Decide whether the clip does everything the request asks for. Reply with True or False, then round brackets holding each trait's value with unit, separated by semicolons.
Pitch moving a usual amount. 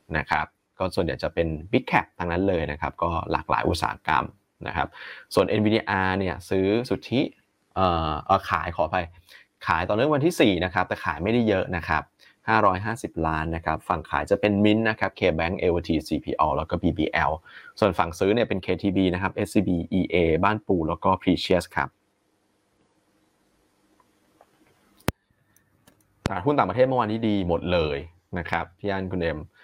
True (3.7 semitones)